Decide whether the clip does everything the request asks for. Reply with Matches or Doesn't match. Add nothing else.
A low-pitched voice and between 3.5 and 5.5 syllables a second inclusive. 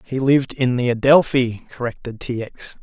Matches